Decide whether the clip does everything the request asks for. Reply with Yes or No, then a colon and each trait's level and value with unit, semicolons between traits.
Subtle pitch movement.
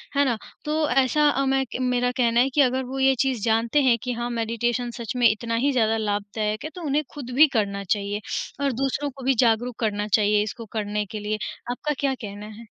No: average, 3.7 semitones